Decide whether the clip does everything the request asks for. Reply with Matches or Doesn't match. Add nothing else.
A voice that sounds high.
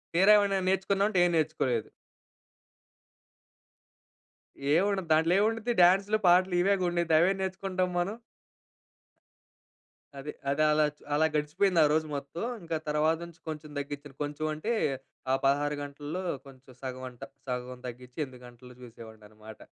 Doesn't match